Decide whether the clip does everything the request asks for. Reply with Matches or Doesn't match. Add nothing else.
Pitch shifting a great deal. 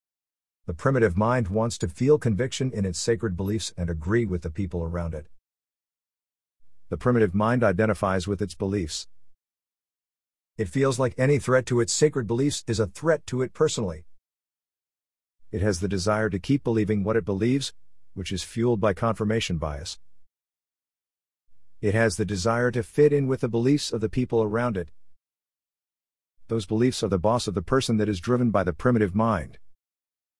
Doesn't match